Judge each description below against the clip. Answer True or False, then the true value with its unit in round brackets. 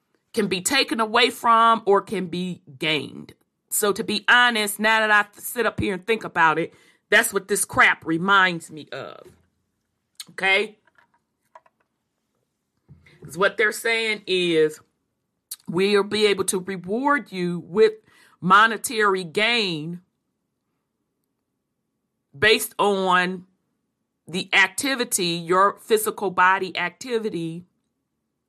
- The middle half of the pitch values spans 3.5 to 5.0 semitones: True (3.9 semitones)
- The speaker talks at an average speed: False (110 wpm)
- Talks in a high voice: True (195 Hz)